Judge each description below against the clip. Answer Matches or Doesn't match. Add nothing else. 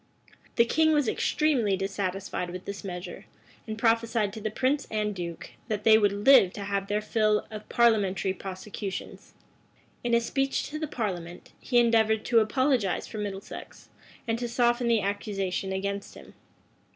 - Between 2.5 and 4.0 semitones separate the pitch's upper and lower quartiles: Matches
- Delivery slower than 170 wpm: Matches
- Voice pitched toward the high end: Matches